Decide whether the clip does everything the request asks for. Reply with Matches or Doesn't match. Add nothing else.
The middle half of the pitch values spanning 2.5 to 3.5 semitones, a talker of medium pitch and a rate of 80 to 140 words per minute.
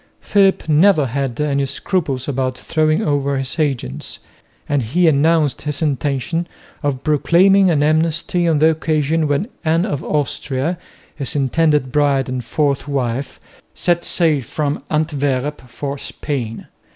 Matches